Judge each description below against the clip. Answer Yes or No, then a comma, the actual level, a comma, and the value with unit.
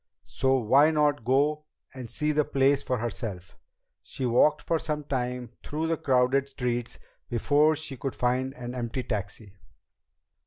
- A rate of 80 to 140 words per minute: No, average, 150 wpm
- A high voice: No, low, 130 Hz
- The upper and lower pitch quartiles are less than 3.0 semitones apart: No, average, 3.3 semitones